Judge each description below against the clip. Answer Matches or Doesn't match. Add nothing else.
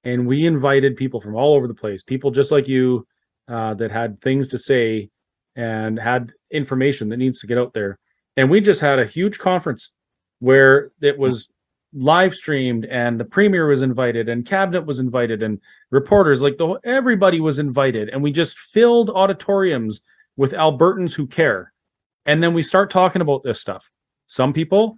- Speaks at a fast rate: Doesn't match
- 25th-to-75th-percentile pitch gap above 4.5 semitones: Matches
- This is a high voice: Doesn't match